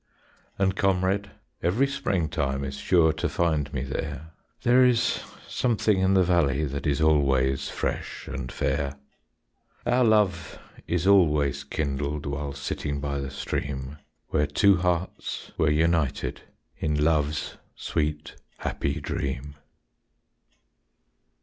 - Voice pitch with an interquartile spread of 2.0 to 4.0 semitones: No, average, 4.7 semitones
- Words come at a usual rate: No, slow, 120 wpm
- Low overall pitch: Yes, very low, 75 Hz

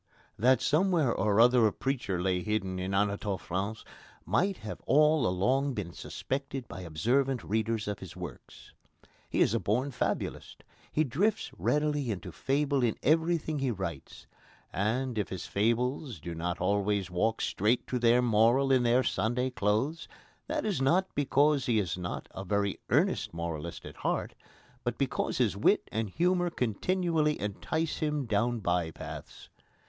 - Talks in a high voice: No, low, 120 Hz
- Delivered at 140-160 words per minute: Yes, average, 155 wpm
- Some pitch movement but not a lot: No, wide, 5.8 semitones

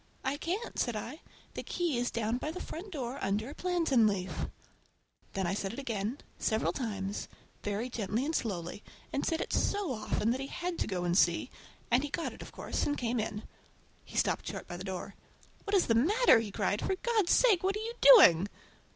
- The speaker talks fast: Yes, fast, 215 wpm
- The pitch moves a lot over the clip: Yes, wide, 8.5 semitones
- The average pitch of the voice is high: Yes, high, 245 Hz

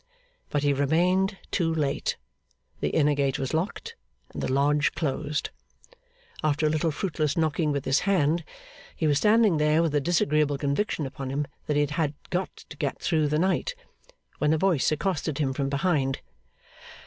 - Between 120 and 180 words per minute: Yes, average, 170 wpm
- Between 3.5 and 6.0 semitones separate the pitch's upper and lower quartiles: No, average, 2.7 semitones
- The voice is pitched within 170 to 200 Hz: No, medium, 150 Hz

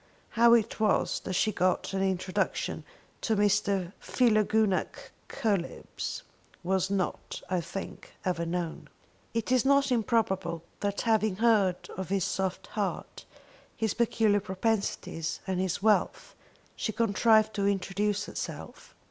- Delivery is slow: Yes, slow, 125 wpm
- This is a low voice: No, high, 200 Hz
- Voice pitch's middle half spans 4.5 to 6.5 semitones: No, average, 2.8 semitones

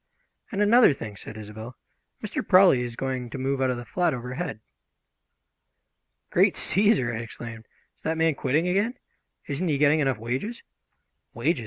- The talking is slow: No, average, 160 wpm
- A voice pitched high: No, low, 135 Hz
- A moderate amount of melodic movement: No, wide, 6.8 semitones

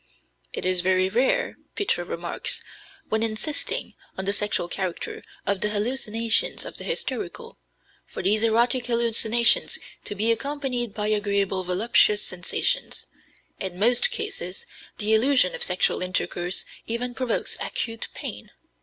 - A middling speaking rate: No, slow, 130 wpm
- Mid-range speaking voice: No, high, 215 Hz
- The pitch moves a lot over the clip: No, average, 4.3 semitones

